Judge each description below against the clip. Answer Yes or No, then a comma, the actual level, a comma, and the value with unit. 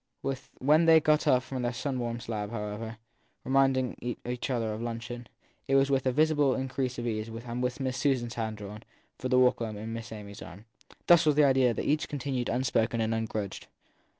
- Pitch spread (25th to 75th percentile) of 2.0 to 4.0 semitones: Yes, average, 2.9 semitones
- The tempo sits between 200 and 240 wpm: Yes, fast, 205 wpm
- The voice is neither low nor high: No, low, 120 Hz